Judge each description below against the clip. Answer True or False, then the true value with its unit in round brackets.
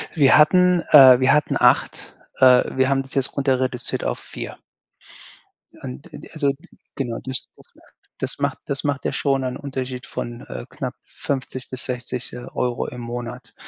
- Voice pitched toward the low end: True (130 Hz)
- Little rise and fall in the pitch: True (2.0 semitones)